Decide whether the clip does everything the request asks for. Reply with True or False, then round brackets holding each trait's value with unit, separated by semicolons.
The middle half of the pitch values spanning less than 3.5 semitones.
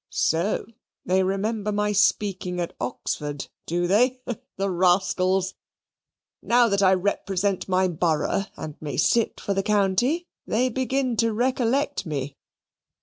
False (3.9 semitones)